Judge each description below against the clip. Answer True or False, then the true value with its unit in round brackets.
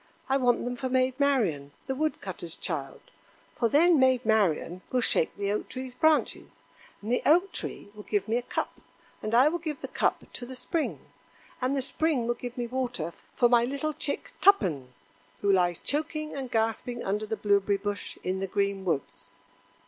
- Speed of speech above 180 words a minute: True (190 wpm)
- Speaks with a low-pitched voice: False (240 Hz)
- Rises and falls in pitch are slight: False (5.1 semitones)